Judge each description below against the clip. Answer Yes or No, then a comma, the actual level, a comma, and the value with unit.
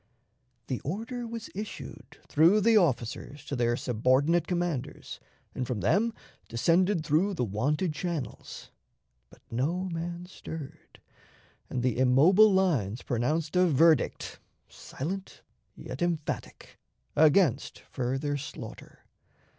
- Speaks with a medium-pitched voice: Yes, medium, 155 Hz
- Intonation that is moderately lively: No, wide, 5.9 semitones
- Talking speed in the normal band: No, slow, 110 wpm